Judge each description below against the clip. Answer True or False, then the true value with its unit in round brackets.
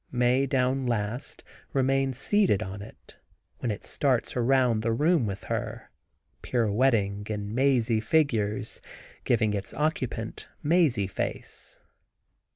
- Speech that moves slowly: True (115 wpm)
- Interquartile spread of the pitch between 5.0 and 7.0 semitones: False (4.0 semitones)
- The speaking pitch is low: True (120 Hz)